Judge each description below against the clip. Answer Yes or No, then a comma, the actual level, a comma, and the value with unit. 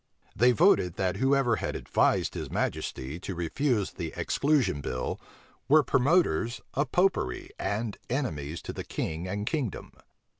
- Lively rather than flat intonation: Yes, wide, 8.4 semitones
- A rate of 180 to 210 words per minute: No, average, 140 wpm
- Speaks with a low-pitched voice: Yes, low, 115 Hz